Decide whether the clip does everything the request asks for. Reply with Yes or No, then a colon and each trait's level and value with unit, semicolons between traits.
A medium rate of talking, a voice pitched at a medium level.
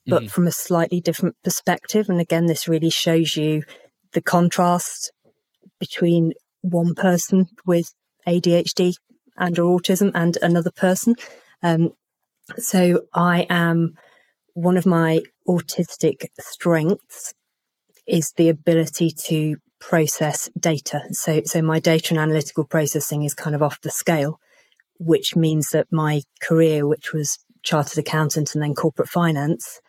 No: slow, 130 wpm; medium, 170 Hz